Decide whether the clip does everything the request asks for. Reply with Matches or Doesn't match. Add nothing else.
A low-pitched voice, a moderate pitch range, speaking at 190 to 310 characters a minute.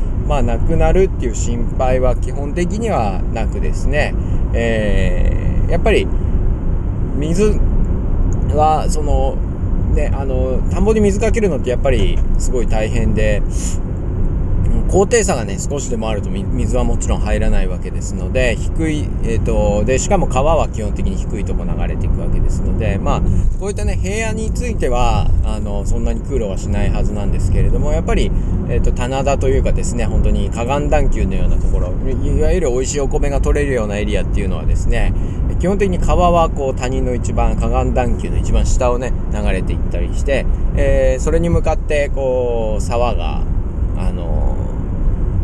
Doesn't match